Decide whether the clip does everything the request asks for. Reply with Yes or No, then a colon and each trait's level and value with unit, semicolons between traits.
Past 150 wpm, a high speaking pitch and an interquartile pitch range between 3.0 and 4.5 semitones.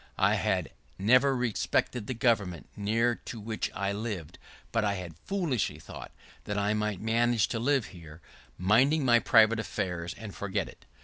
No: average, 165 wpm; low, 110 Hz; average, 3.3 semitones